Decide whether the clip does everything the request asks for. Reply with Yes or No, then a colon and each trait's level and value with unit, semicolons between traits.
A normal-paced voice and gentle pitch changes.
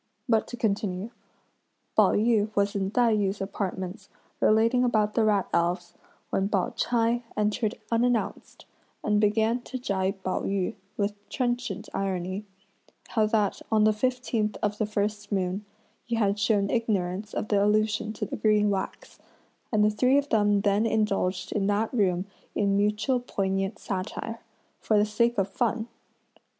Yes: average, 155 wpm; narrow, 2.2 semitones